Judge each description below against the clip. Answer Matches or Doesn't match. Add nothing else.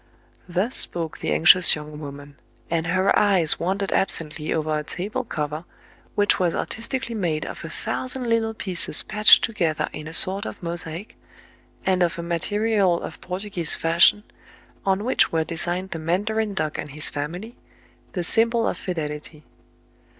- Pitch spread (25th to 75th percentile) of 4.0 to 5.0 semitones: Matches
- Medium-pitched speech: Matches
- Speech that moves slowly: Doesn't match